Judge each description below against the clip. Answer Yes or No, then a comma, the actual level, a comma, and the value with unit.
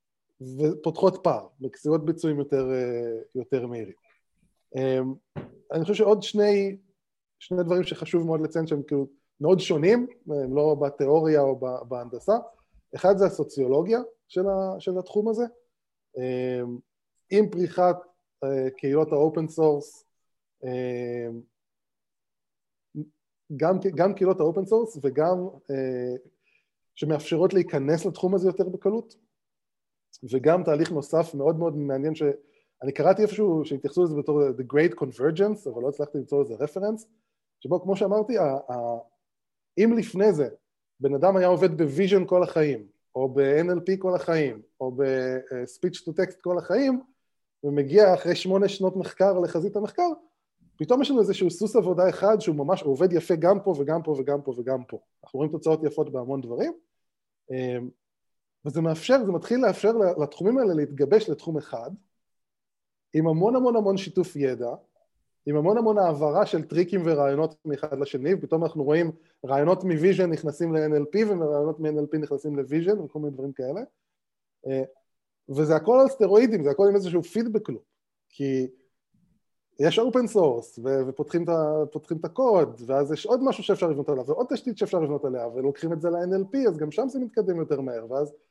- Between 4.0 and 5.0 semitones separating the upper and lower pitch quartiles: No, wide, 5.5 semitones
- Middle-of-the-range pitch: Yes, medium, 160 Hz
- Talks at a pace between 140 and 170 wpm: Yes, average, 145 wpm